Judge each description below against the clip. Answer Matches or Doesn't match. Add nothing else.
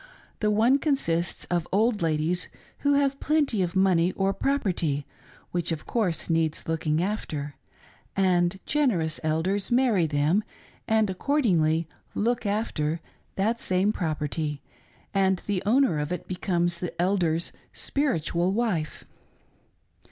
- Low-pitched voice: Doesn't match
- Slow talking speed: Matches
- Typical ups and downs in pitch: Matches